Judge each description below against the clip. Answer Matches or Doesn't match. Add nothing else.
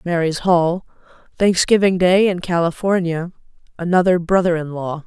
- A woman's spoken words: Matches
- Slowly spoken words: Matches